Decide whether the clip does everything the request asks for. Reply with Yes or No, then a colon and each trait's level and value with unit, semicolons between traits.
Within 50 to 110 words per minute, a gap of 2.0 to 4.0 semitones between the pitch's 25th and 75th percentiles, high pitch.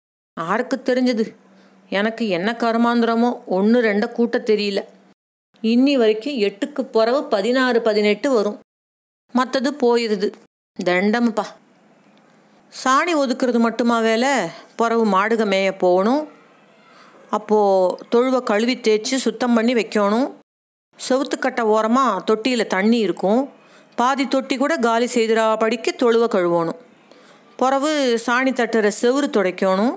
Yes: average, 100 wpm; average, 3.2 semitones; high, 230 Hz